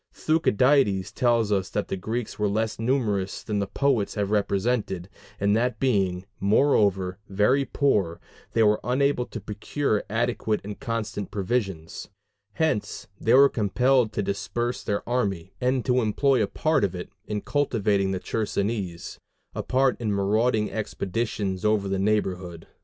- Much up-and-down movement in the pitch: No, average, 3.8 semitones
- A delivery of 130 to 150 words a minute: Yes, average, 145 wpm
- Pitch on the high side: No, low, 105 Hz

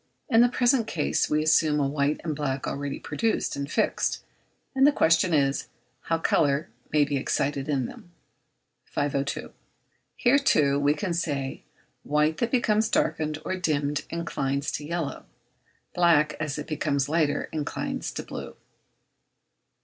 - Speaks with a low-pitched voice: No, medium, 150 Hz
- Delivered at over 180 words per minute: No, average, 145 wpm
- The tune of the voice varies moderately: Yes, average, 3.1 semitones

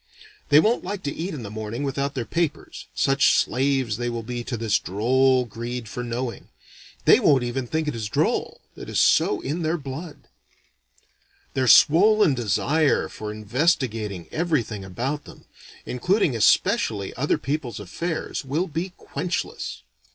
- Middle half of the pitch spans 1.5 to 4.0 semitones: No, average, 5.2 semitones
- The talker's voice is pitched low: Yes, low, 130 Hz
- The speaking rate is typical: Yes, average, 150 wpm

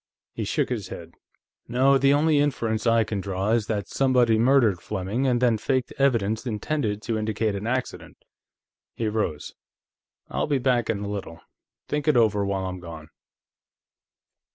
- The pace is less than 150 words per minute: No, average, 160 wpm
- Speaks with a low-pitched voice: Yes, low, 115 Hz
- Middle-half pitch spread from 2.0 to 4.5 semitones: Yes, average, 4.1 semitones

